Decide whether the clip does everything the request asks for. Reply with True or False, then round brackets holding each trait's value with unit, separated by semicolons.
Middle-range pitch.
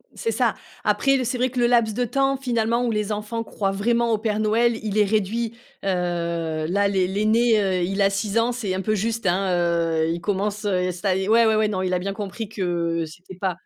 False (205 Hz)